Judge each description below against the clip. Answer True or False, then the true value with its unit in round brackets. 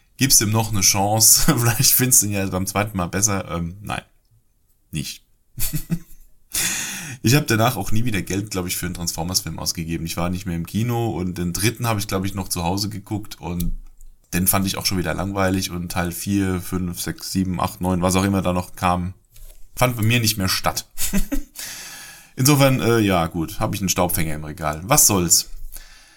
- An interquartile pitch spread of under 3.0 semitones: False (4.1 semitones)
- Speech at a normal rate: False (200 wpm)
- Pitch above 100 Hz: False (95 Hz)